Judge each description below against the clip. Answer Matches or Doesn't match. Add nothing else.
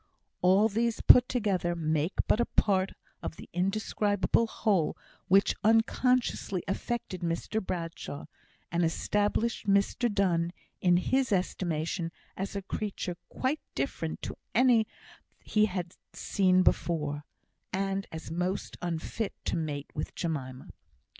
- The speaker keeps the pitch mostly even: Doesn't match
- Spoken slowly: Matches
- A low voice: Doesn't match